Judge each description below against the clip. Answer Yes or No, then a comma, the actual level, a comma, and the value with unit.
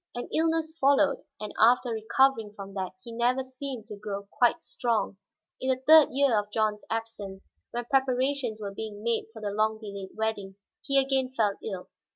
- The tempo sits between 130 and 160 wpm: No, average, 180 wpm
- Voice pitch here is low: No, high, 225 Hz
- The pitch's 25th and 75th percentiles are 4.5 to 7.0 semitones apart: No, average, 4.0 semitones